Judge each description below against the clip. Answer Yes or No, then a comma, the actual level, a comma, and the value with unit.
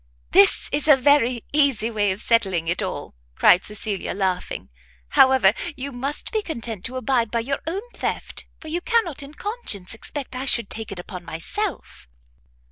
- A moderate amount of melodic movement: No, wide, 6.2 semitones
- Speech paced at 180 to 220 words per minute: No, average, 170 wpm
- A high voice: Yes, high, 245 Hz